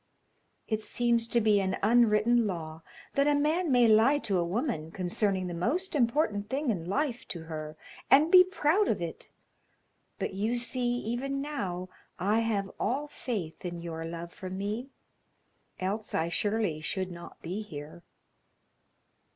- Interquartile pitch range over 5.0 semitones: Yes, wide, 5.6 semitones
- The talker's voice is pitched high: Yes, high, 215 Hz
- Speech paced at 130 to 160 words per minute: Yes, average, 155 wpm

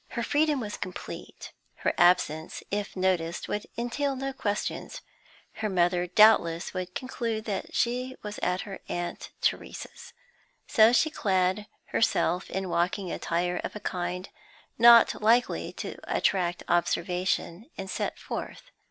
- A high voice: Yes, high, 195 Hz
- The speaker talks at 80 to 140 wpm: Yes, slow, 135 wpm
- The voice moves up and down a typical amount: Yes, average, 4.6 semitones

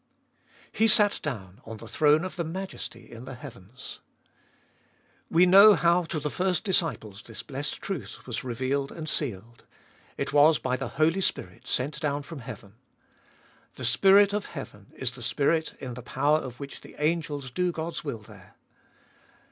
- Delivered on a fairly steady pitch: No, wide, 5.6 semitones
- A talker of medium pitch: Yes, medium, 145 Hz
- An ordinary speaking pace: Yes, average, 170 wpm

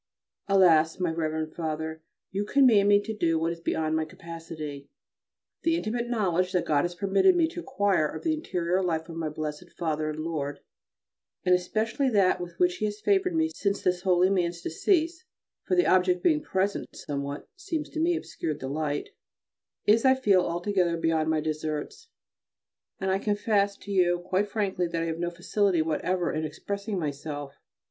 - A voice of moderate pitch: Yes, medium, 180 Hz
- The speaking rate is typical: Yes, average, 180 wpm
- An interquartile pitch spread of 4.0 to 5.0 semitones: Yes, average, 4.5 semitones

